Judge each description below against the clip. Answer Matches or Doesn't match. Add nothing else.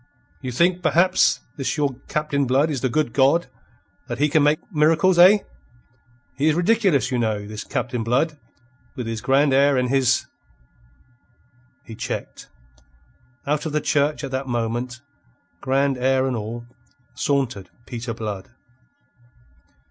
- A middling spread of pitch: Matches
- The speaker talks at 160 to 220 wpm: Doesn't match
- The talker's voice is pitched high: Doesn't match